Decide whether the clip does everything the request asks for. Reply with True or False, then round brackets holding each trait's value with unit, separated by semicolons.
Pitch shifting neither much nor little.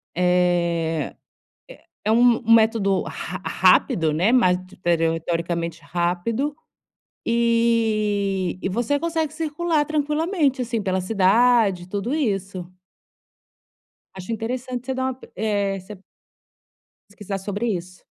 False (5.8 semitones)